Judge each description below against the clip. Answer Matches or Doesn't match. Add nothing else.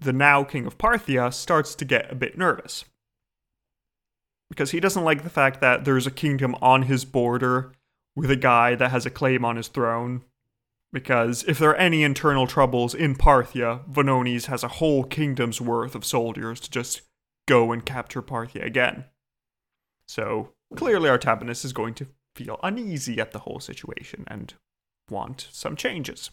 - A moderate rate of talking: Matches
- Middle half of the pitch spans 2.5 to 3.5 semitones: Matches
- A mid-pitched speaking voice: Doesn't match